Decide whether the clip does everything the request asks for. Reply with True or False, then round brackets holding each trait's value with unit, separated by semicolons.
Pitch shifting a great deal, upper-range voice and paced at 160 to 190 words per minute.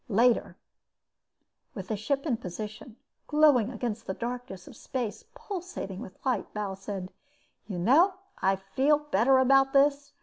False (5.8 semitones; 240 Hz; 140 wpm)